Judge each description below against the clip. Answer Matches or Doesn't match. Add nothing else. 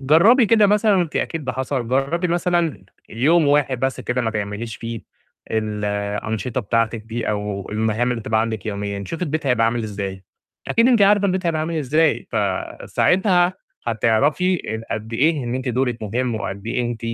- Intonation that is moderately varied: Doesn't match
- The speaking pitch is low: Matches